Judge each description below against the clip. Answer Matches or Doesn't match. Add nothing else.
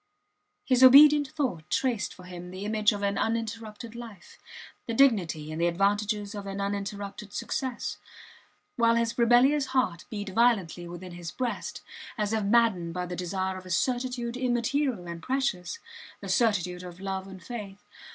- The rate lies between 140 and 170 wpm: Matches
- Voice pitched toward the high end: Matches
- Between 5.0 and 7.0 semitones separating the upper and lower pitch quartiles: Doesn't match